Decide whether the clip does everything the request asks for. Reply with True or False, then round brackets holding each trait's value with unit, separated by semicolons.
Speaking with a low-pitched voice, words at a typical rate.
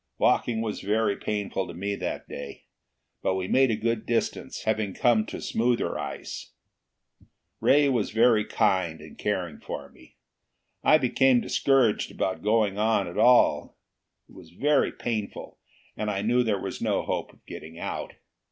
True (110 Hz; 160 wpm)